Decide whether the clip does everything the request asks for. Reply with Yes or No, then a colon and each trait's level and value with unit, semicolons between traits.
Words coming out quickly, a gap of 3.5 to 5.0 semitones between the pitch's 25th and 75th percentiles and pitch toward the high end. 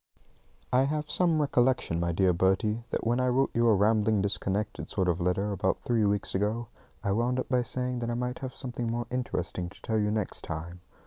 No: fast, 210 wpm; average, 4.3 semitones; low, 110 Hz